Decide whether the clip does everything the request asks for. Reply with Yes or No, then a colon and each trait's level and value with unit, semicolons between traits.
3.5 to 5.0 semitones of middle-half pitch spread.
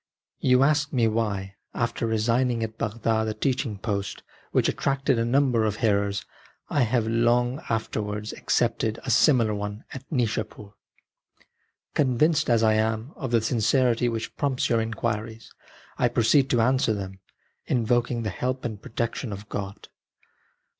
No: narrow, 2.6 semitones